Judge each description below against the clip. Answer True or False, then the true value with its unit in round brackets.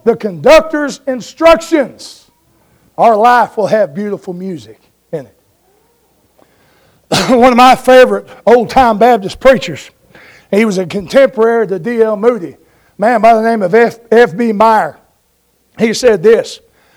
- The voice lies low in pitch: False (230 Hz)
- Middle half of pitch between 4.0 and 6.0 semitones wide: False (3.2 semitones)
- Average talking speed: False (130 wpm)